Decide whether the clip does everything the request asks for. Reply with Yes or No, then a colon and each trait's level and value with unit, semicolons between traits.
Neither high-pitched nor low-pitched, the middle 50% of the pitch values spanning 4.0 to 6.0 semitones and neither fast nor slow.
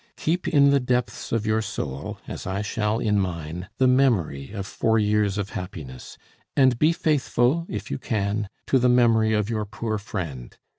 No: low, 110 Hz; average, 4.3 semitones; average, 180 wpm